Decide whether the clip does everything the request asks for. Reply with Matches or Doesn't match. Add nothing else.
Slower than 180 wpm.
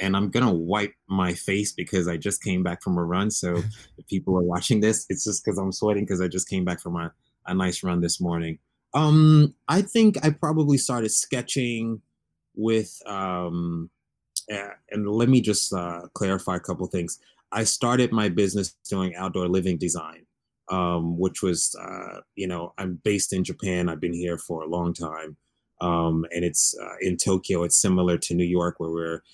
Doesn't match